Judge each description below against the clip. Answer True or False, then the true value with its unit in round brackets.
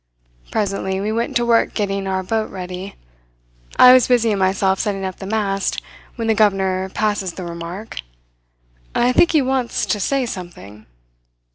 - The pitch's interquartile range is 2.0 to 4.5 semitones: True (3.0 semitones)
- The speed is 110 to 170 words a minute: True (155 wpm)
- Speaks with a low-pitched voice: False (200 Hz)